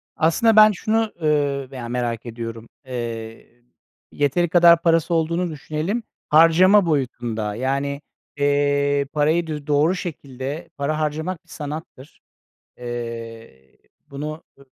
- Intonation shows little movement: No, average, 4.9 semitones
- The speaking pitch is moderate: Yes, medium, 145 Hz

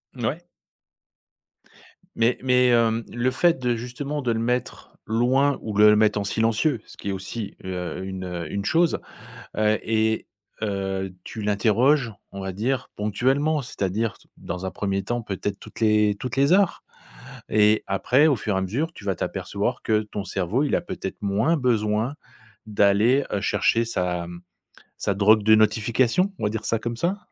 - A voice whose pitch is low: Yes, low, 110 Hz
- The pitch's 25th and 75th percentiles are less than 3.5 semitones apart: No, average, 3.9 semitones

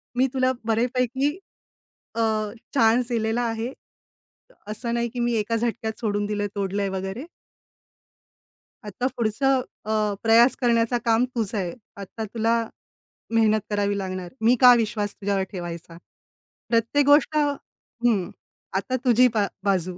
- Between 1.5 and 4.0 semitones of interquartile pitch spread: Yes, average, 2.8 semitones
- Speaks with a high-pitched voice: Yes, high, 225 Hz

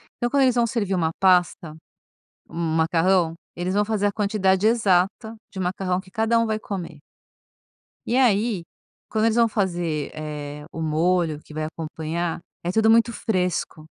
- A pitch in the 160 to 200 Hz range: Yes, medium, 185 Hz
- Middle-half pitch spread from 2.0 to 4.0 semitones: No, average, 5.0 semitones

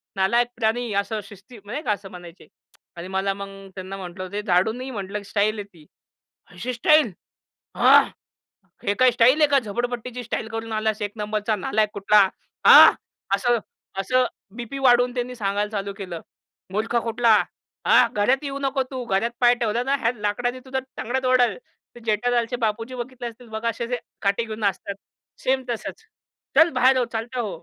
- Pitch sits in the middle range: No, high, 225 Hz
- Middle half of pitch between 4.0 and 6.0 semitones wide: No, average, 3.4 semitones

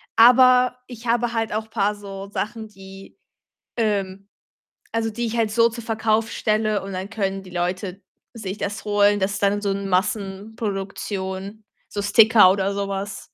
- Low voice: No, high, 205 Hz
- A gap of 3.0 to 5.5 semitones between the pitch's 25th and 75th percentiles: No, narrow, 2.4 semitones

